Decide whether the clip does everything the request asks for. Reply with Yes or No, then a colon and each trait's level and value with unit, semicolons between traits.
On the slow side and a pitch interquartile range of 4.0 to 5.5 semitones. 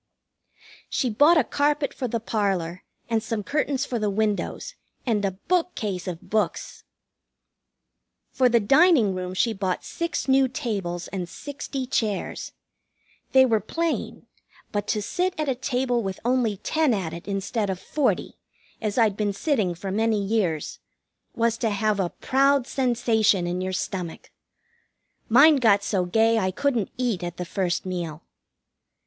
No: average, 155 wpm; average, 5.2 semitones